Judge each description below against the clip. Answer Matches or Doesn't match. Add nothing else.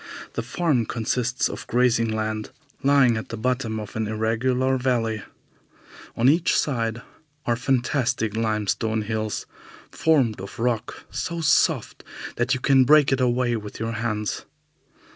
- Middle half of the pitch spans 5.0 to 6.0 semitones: Doesn't match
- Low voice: Matches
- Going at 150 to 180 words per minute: Doesn't match